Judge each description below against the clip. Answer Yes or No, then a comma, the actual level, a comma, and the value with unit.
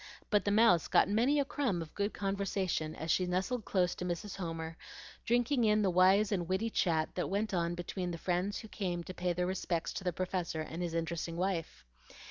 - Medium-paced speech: No, fast, 210 wpm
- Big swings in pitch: No, average, 3.0 semitones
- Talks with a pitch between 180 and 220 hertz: Yes, medium, 185 Hz